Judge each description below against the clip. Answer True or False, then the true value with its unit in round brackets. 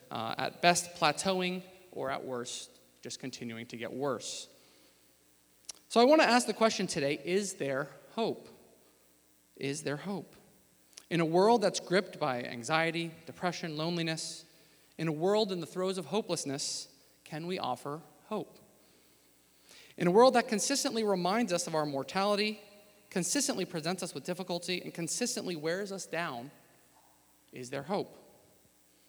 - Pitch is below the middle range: False (170 Hz)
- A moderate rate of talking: True (145 wpm)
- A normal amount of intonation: False (5.8 semitones)